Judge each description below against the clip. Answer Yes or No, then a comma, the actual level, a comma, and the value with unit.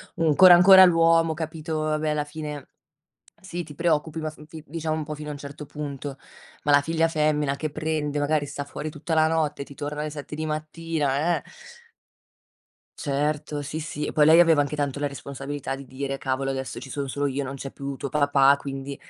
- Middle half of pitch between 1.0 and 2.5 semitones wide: Yes, narrow, 1.9 semitones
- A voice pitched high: No, medium, 150 Hz